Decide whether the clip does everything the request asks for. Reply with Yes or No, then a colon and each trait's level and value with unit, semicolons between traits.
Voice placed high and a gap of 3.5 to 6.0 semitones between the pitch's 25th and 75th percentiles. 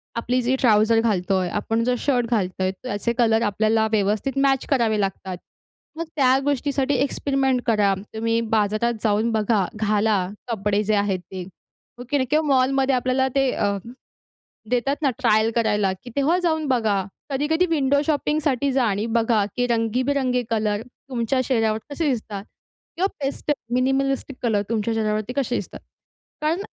Yes: high, 235 Hz; average, 4.1 semitones